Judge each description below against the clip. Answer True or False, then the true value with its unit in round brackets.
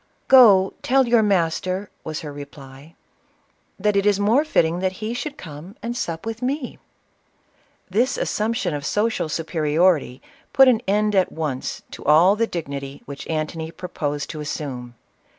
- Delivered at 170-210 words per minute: False (155 wpm)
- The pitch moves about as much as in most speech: False (6.2 semitones)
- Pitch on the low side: False (180 Hz)